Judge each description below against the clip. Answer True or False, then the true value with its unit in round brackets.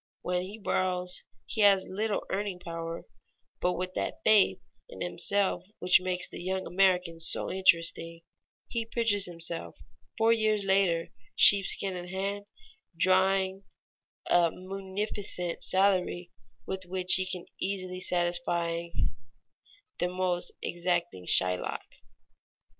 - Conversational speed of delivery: False (115 wpm)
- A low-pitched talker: False (185 Hz)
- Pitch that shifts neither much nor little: False (1.9 semitones)